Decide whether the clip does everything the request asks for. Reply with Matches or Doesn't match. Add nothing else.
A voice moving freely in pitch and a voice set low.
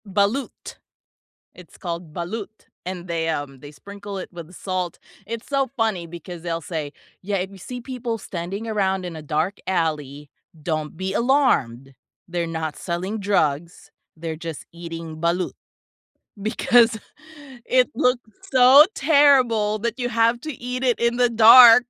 Doesn't match